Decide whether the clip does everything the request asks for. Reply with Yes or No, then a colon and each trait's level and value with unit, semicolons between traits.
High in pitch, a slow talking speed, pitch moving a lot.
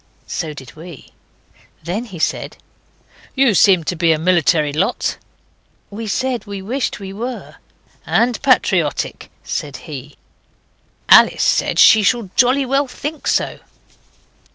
Yes: high, 195 Hz; slow, 130 wpm; wide, 7.2 semitones